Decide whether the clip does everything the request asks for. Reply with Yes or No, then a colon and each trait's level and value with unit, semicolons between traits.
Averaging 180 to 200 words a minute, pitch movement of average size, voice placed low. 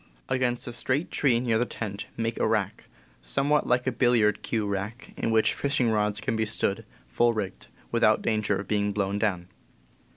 Yes: average, 185 wpm; average, 3.0 semitones; low, 110 Hz